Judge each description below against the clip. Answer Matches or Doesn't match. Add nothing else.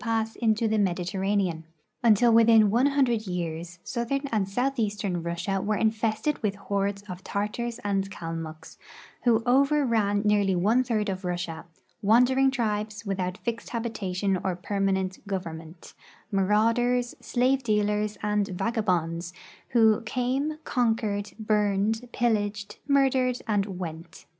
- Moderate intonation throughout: Matches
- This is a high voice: Matches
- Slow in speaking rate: Matches